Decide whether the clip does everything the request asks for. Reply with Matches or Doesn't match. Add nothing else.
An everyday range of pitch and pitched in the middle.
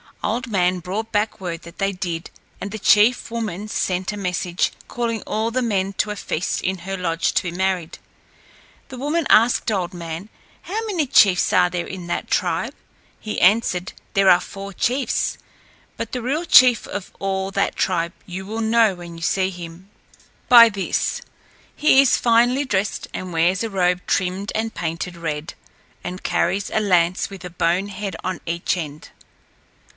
Doesn't match